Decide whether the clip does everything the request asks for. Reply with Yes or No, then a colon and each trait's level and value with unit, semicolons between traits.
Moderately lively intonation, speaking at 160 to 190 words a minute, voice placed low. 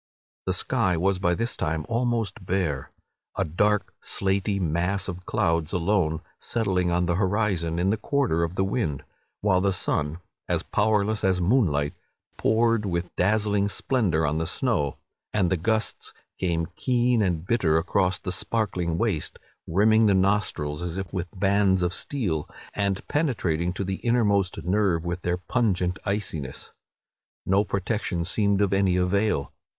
No: average, 3.3 semitones; average, 150 wpm; very low, 95 Hz